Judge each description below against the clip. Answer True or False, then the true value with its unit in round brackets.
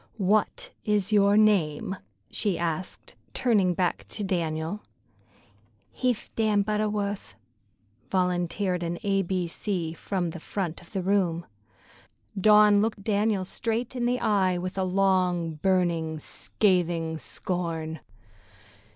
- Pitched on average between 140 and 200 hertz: True (190 Hz)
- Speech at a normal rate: False (115 wpm)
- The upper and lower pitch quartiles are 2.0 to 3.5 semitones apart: True (3.2 semitones)